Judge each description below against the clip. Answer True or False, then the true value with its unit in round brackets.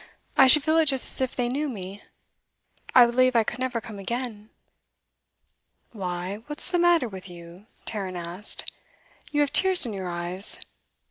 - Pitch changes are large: True (6.0 semitones)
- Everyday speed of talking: True (170 wpm)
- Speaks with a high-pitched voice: True (230 Hz)